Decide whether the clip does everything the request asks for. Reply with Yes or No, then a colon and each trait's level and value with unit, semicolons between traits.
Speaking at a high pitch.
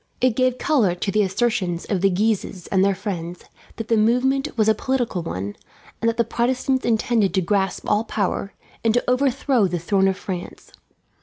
Yes: high, 215 Hz